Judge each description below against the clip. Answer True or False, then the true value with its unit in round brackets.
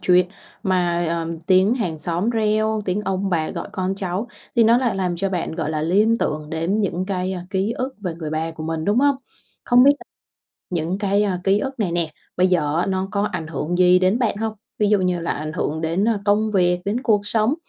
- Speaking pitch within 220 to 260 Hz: False (185 Hz)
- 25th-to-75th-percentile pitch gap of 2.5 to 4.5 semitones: True (3.8 semitones)